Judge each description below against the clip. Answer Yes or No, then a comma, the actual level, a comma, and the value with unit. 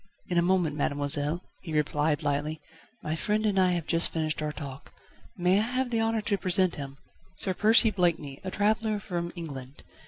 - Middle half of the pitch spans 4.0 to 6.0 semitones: Yes, average, 5.2 semitones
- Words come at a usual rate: Yes, average, 185 wpm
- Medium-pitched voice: Yes, medium, 175 Hz